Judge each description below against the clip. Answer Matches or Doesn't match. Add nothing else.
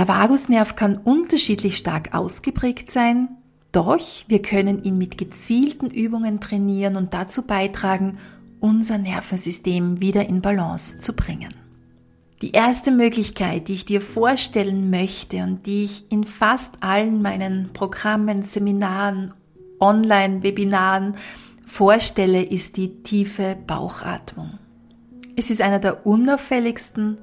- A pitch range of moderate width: Matches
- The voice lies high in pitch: Matches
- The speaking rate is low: Matches